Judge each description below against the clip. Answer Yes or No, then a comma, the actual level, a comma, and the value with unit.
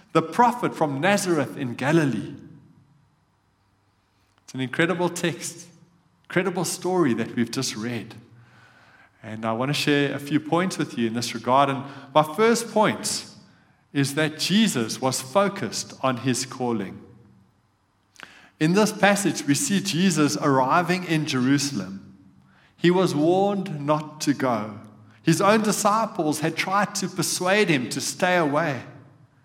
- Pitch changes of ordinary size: No, wide, 6.4 semitones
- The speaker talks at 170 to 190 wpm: No, slow, 135 wpm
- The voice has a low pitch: No, medium, 150 Hz